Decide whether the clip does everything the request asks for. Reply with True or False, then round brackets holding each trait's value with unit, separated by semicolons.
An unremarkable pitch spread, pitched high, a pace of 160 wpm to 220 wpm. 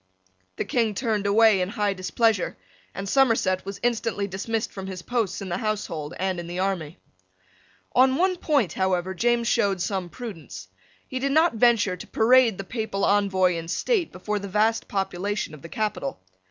True (3.7 semitones; 200 Hz; 175 wpm)